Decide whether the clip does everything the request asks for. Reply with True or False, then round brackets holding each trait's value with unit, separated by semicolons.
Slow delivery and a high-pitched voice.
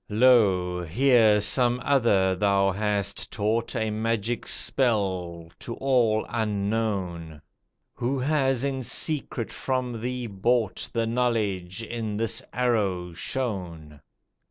False (110 wpm; 110 Hz)